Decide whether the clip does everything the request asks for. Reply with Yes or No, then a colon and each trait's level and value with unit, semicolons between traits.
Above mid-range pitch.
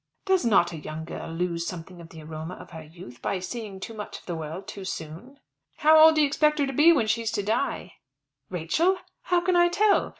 Yes: high, 200 Hz